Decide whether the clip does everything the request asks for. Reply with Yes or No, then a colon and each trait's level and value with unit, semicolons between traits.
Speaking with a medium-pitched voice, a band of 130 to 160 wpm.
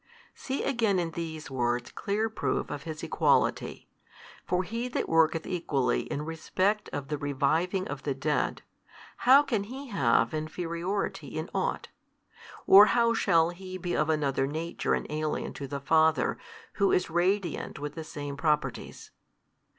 Yes: medium, 165 Hz; average, 150 wpm